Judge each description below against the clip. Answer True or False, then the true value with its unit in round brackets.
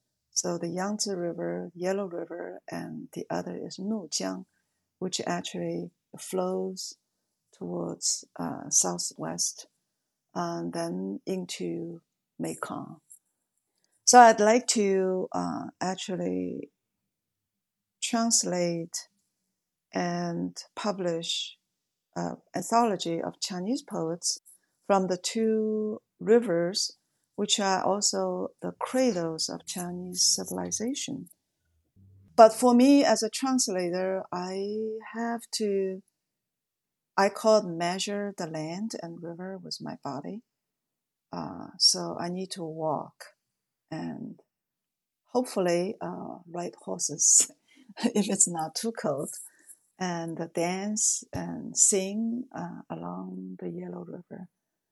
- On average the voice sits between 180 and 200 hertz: True (185 Hz)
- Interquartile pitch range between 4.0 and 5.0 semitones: True (4.7 semitones)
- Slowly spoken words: True (100 wpm)